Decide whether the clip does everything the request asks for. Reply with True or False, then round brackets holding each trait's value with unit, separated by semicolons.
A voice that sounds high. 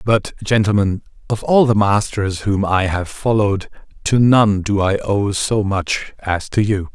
False (105 Hz)